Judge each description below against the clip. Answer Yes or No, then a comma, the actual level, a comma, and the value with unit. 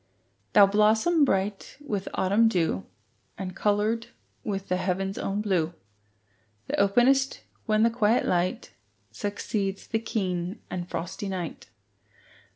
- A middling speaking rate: No, slow, 120 wpm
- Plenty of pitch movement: No, average, 3.0 semitones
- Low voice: No, high, 200 Hz